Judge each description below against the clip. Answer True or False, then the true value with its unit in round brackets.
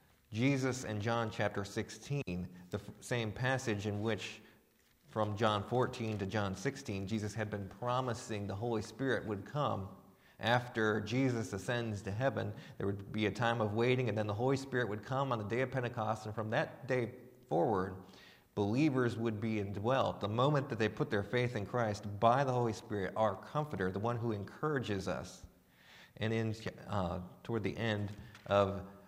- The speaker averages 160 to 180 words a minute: True (175 wpm)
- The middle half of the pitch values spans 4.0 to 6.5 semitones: False (3.3 semitones)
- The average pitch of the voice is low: True (110 Hz)